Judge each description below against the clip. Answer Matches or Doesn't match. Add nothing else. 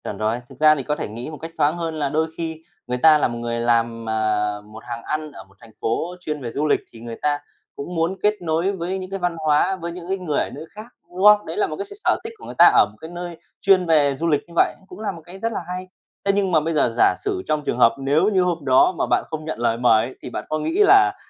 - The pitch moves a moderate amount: Doesn't match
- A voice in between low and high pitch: Matches